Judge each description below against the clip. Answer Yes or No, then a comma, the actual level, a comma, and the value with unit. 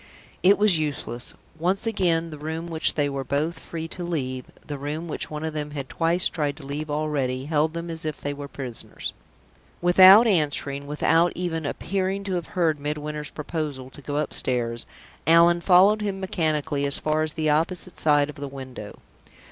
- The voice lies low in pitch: No, medium, 155 Hz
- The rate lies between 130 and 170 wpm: No, average, 180 wpm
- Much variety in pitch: No, average, 3.1 semitones